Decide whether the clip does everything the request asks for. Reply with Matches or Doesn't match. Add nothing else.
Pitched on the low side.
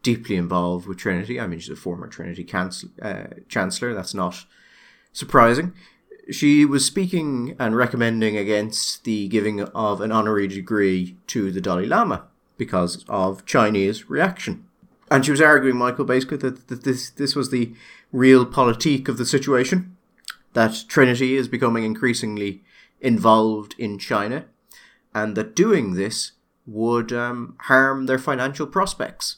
Matches